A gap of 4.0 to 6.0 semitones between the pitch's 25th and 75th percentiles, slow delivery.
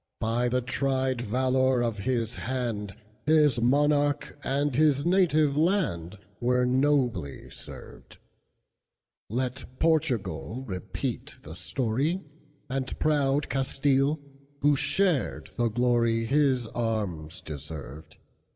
Yes: average, 4.3 semitones; slow, 85 wpm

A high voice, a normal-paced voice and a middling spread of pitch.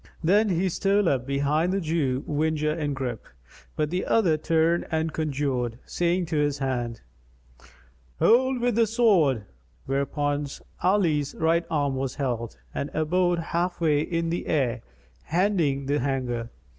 No: medium, 155 Hz; average, 145 wpm; average, 4.1 semitones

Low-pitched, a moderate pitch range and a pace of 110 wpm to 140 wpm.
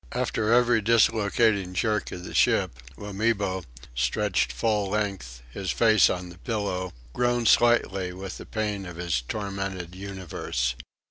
Yes: low, 100 Hz; average, 3.2 semitones; slow, 135 wpm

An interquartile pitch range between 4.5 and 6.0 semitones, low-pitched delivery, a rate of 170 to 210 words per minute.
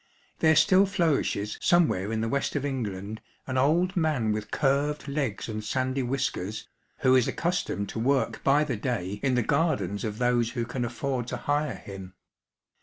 Yes: average, 5.0 semitones; low, 130 Hz; average, 175 wpm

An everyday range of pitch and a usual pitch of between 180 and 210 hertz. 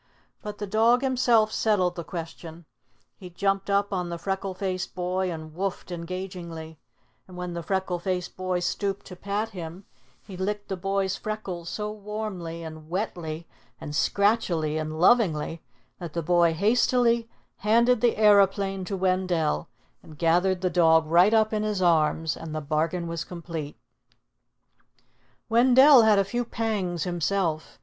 Yes: average, 3.7 semitones; medium, 185 Hz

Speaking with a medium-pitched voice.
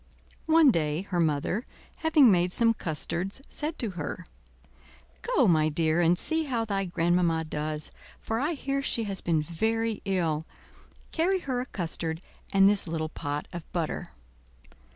Yes: medium, 180 Hz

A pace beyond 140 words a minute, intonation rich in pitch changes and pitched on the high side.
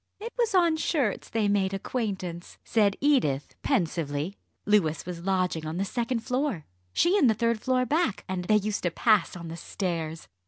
Yes: average, 180 wpm; wide, 6.5 semitones; high, 205 Hz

